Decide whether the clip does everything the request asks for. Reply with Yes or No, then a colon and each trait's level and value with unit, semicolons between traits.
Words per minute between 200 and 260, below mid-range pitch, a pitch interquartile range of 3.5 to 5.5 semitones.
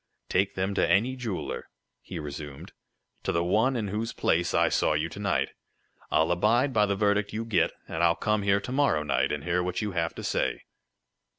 Yes: fast, 205 wpm; low, 100 Hz; average, 4.2 semitones